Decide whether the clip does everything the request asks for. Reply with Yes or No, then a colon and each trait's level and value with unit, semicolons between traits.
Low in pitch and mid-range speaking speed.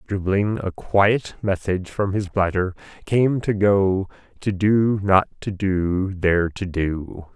Yes: very low, 95 Hz; average, 145 wpm